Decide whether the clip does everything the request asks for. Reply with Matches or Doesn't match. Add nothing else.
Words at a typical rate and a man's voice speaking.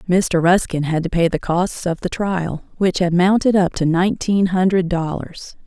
Doesn't match